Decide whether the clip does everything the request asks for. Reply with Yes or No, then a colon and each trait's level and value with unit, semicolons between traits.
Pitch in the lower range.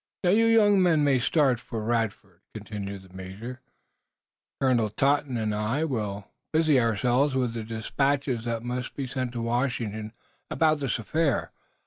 Yes: low, 120 Hz